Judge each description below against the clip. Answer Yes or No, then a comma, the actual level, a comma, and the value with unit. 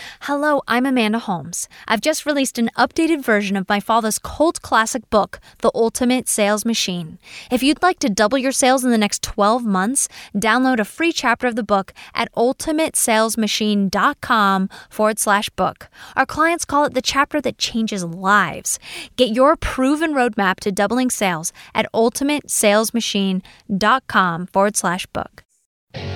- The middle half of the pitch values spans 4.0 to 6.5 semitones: Yes, average, 4.4 semitones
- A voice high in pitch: Yes, high, 230 Hz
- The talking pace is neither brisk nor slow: Yes, average, 150 wpm